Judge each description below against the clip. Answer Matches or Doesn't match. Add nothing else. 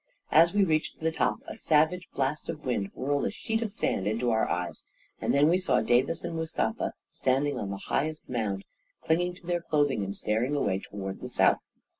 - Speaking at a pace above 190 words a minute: Matches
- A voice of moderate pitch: Matches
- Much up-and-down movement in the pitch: Matches